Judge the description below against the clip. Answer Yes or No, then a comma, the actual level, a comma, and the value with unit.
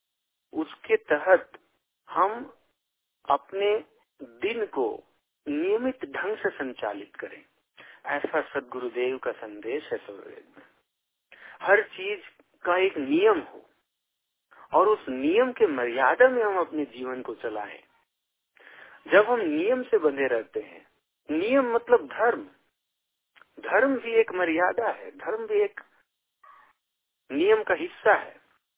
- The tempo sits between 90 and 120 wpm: Yes, average, 115 wpm